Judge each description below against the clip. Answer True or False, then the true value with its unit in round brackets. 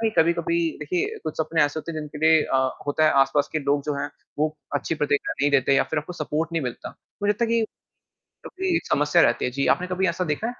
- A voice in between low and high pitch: True (155 Hz)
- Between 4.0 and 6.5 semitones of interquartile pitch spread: False (2.8 semitones)